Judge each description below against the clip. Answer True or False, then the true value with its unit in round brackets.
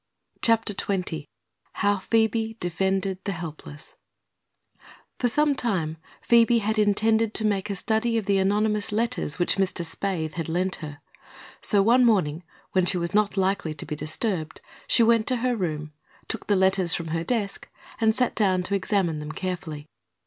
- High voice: True (195 Hz)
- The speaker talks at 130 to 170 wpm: True (165 wpm)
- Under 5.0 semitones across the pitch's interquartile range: True (4.4 semitones)